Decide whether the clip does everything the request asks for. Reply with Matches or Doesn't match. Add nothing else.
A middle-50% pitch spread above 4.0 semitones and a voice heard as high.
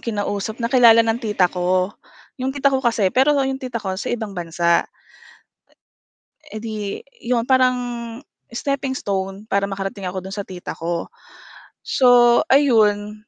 Matches